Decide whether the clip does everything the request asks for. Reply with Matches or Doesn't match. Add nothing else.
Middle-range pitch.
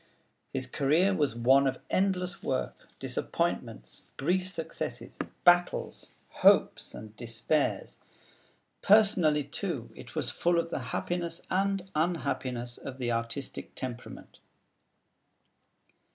Matches